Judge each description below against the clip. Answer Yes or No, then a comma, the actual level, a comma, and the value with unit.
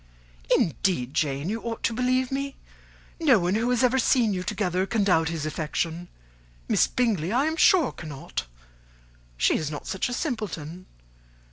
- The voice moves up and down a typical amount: No, wide, 7.3 semitones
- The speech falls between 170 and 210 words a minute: No, average, 160 wpm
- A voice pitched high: Yes, high, 200 Hz